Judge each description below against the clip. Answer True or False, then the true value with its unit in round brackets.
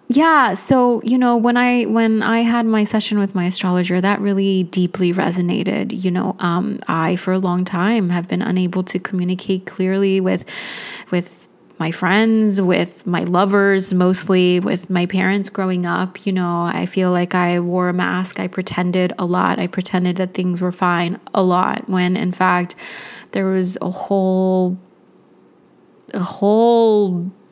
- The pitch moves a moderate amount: False (2.0 semitones)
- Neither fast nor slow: True (165 wpm)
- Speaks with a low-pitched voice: False (185 Hz)